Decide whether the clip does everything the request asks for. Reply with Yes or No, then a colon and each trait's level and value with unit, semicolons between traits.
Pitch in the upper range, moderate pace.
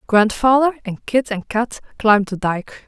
Yes: high, 225 Hz; average, 165 wpm